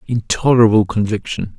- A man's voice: Yes, male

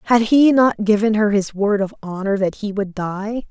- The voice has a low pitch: No, high, 210 Hz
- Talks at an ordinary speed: No, fast, 225 wpm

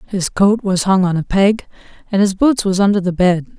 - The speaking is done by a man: No, female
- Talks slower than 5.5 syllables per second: Yes, 5.1 syllables/s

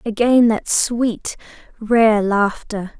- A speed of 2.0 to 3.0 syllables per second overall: Yes, 2.9 syllables/s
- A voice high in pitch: Yes, high, 225 Hz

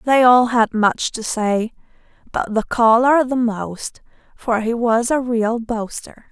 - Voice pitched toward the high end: Yes, high, 230 Hz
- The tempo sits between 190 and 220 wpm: No, average, 160 wpm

